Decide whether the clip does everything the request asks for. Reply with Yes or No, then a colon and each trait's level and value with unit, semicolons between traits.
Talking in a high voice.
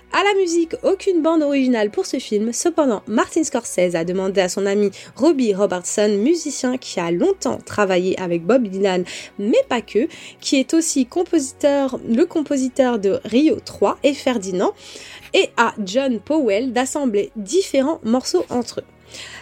Yes: very high, 255 Hz